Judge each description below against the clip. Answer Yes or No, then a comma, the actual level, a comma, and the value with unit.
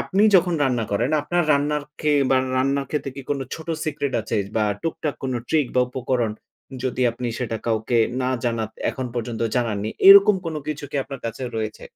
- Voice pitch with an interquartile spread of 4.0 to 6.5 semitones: Yes, average, 4.3 semitones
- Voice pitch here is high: No, low, 130 Hz